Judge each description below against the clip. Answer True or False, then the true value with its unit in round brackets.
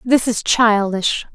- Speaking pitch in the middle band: False (220 Hz)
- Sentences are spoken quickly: False (135 wpm)